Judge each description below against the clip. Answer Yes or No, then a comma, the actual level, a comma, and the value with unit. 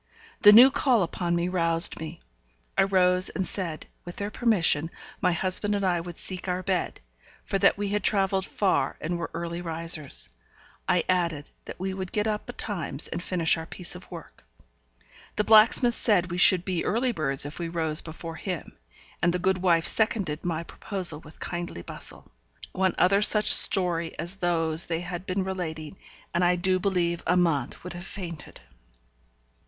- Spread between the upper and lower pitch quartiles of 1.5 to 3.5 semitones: Yes, narrow, 2.5 semitones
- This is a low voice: No, medium, 180 Hz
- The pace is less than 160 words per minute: No, average, 175 wpm